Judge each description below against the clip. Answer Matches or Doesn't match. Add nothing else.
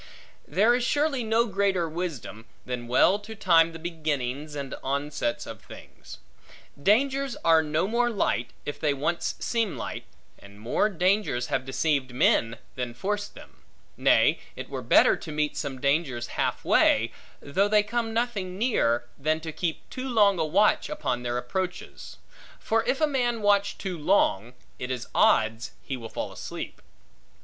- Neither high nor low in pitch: Matches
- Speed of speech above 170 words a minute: Doesn't match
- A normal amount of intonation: Doesn't match